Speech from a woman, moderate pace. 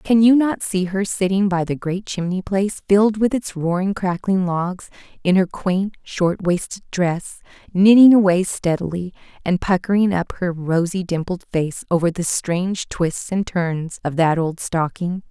Yes: female; average, 170 wpm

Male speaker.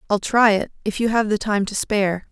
No: female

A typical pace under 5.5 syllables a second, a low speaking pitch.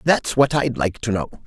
Yes: 4.9 syllables/s; low, 120 Hz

